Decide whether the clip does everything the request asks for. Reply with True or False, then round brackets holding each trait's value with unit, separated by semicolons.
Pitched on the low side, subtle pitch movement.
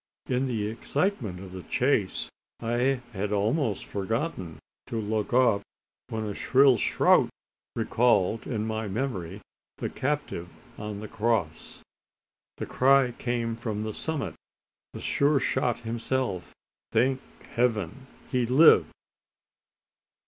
False (115 Hz; 3.7 semitones)